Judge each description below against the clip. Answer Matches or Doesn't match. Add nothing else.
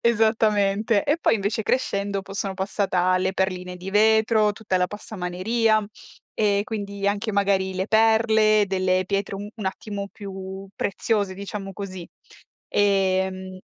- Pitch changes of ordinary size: Doesn't match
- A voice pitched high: Matches